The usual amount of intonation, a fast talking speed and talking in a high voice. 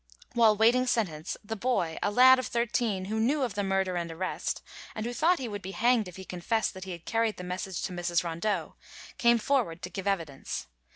Yes: average, 4.6 semitones; fast, 220 wpm; high, 205 Hz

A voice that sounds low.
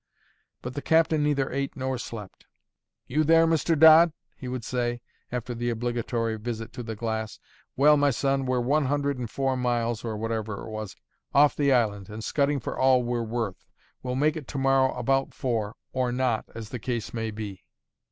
Yes: low, 125 Hz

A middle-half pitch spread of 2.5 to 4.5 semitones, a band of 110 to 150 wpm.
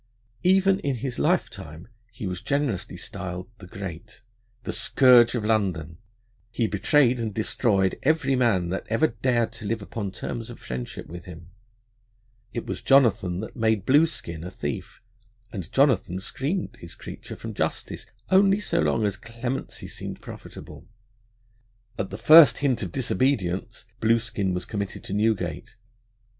No: wide, 5.6 semitones; average, 145 wpm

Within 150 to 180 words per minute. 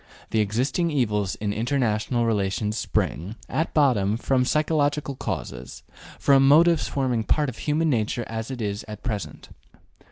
No: average, 140 wpm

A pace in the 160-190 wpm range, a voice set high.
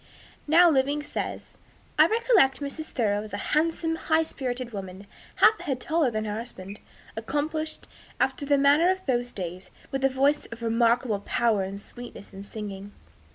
Yes: average, 165 wpm; very high, 255 Hz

